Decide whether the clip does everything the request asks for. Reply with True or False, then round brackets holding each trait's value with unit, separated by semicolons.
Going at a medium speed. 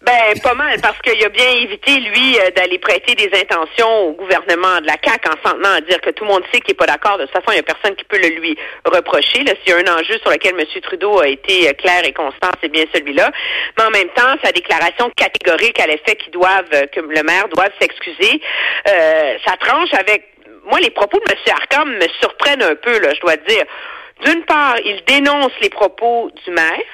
False (230 wpm)